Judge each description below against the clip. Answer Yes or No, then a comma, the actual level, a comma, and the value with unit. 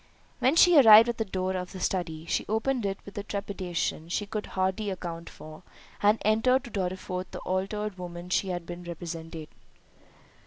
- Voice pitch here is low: No, high, 190 Hz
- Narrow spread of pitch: No, average, 3.3 semitones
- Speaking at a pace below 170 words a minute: No, average, 180 wpm